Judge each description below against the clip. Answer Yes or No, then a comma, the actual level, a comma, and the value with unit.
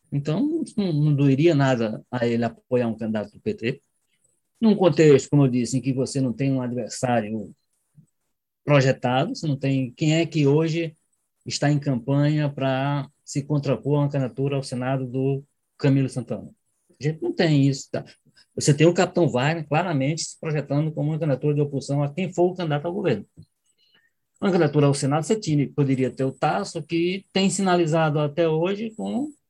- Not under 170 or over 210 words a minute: Yes, average, 175 wpm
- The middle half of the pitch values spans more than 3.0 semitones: Yes, average, 3.7 semitones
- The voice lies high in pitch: No, medium, 145 Hz